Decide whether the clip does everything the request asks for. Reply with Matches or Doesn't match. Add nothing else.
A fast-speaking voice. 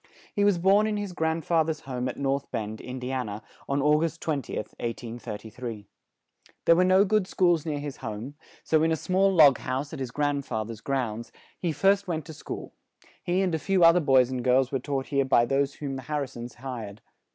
Matches